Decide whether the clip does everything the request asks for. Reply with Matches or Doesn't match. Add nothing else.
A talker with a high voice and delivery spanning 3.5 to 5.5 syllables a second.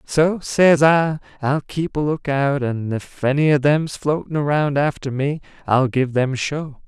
Doesn't match